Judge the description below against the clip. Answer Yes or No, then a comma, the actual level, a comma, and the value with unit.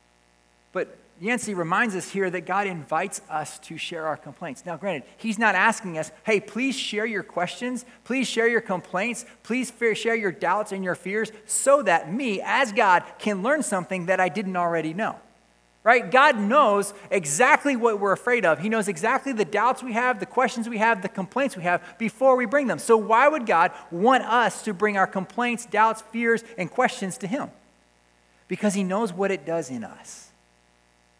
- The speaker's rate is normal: Yes, average, 190 wpm